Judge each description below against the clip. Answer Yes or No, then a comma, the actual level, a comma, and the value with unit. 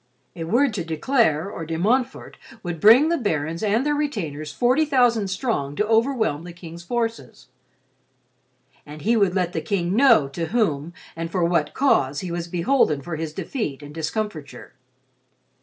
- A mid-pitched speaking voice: Yes, medium, 180 Hz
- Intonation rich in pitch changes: Yes, wide, 6.5 semitones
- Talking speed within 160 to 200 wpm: Yes, average, 170 wpm